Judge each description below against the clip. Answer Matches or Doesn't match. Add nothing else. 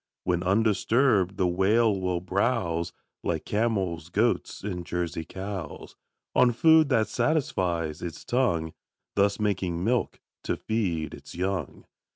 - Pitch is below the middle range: Matches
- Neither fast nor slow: Doesn't match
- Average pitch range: Matches